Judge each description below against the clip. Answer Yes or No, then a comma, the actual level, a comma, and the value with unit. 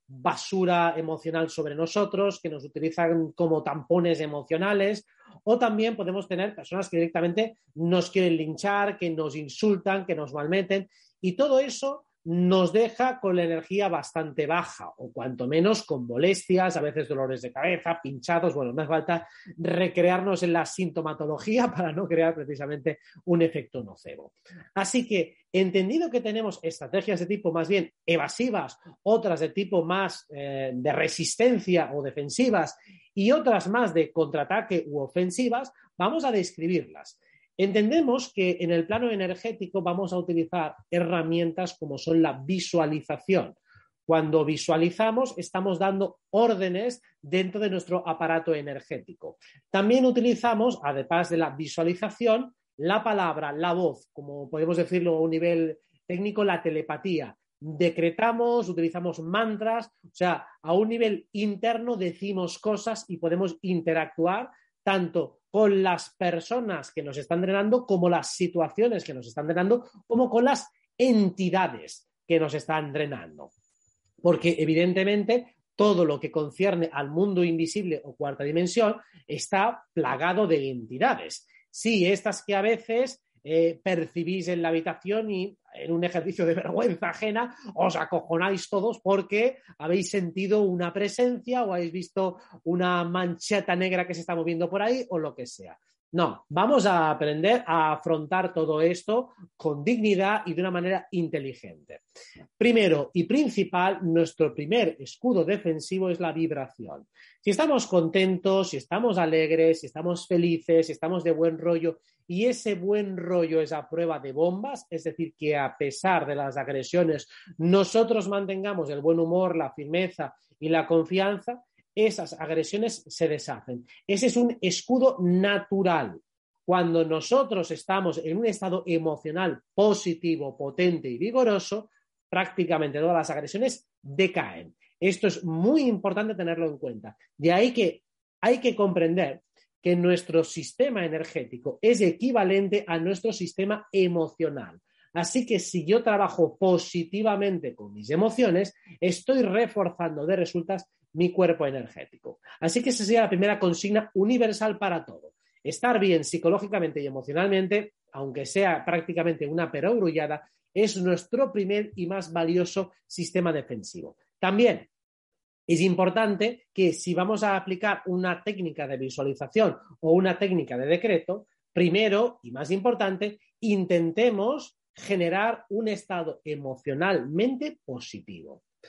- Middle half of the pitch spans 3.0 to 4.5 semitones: Yes, average, 4.0 semitones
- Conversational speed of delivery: Yes, average, 140 wpm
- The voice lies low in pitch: No, medium, 180 Hz